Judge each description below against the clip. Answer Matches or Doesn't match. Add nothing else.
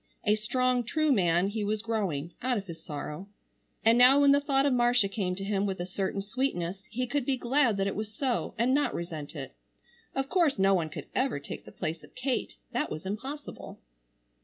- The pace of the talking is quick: Matches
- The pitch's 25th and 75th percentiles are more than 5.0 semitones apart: Matches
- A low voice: Doesn't match